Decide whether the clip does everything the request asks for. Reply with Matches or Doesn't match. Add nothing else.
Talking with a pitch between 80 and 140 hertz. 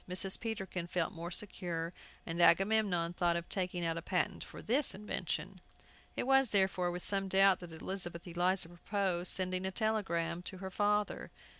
Doesn't match